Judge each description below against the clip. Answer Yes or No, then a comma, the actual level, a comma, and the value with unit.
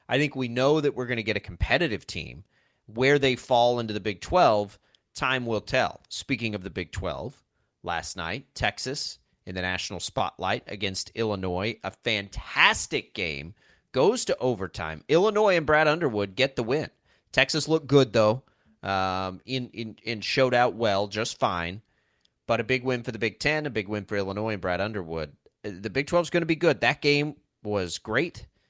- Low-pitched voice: Yes, low, 115 Hz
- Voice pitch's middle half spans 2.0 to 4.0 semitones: No, average, 4.6 semitones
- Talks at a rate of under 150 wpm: No, average, 185 wpm